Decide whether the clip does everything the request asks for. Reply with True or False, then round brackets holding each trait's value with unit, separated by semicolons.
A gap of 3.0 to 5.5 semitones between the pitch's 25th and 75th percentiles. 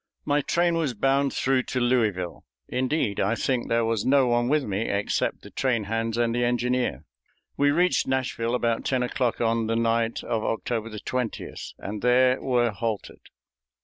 False (2.4 semitones)